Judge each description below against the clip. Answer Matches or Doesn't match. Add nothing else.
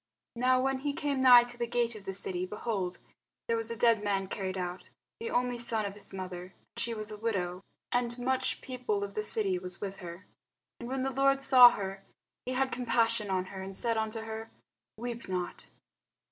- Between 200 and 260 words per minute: Matches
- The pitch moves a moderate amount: Matches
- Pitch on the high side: Matches